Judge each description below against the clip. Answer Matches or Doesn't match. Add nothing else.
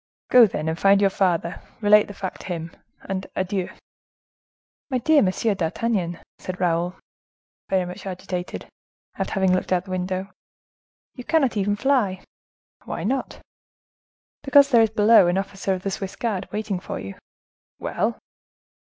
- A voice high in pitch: Matches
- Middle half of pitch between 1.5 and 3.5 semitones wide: Matches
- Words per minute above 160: Doesn't match